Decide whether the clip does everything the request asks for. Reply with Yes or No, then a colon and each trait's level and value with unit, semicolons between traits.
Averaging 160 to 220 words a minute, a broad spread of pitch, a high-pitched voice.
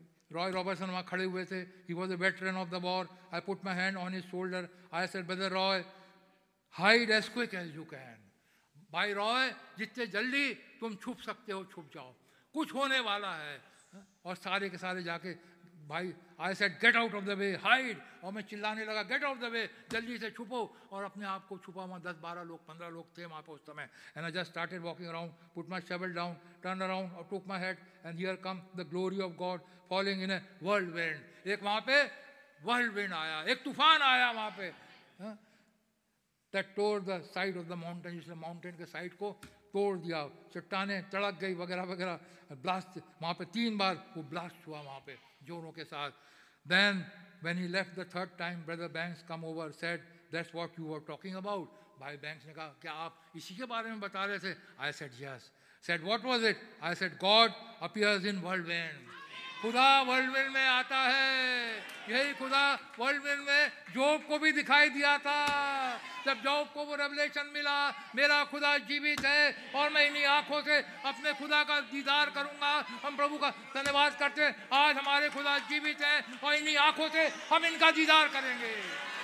Yes: average, 180 wpm; wide, 7.0 semitones; high, 195 Hz